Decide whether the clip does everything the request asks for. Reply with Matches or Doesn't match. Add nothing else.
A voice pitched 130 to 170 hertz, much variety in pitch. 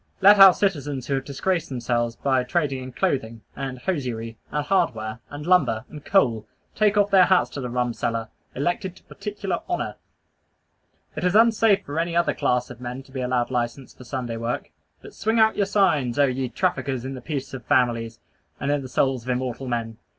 Matches